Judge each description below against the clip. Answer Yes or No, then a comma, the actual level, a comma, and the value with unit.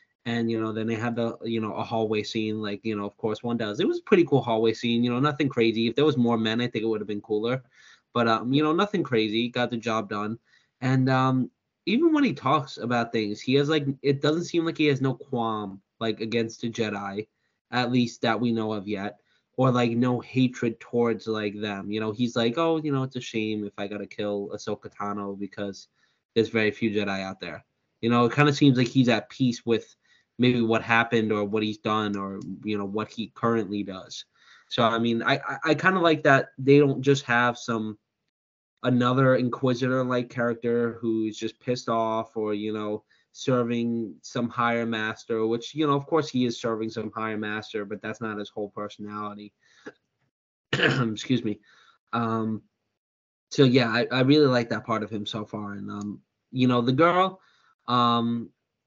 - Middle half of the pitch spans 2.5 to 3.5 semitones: Yes, average, 2.8 semitones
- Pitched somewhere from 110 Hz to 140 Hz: Yes, low, 115 Hz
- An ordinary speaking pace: No, fast, 210 wpm